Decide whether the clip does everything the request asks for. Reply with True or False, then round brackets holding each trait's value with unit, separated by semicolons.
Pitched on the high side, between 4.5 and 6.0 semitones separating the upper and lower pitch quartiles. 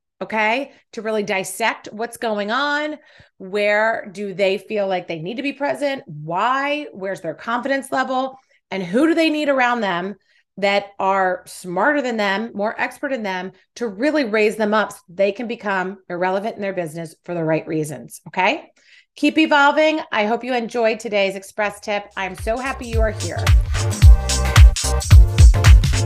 True (205 Hz; 5.2 semitones)